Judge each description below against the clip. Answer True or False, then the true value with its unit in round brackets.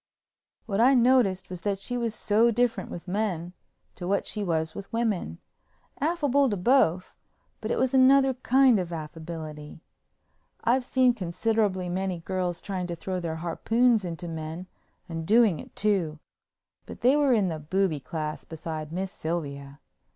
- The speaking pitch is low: False (190 Hz)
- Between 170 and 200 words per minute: False (155 wpm)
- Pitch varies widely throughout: True (5.9 semitones)